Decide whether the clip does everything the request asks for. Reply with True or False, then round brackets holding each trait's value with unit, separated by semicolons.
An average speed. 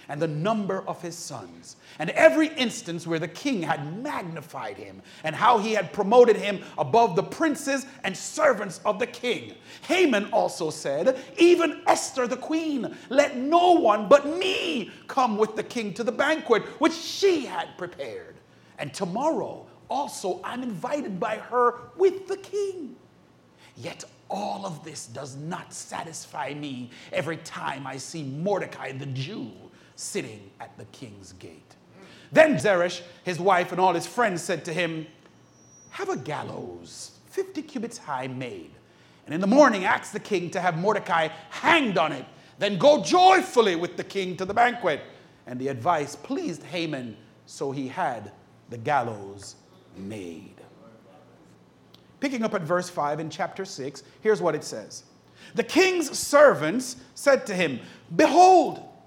True (155 wpm)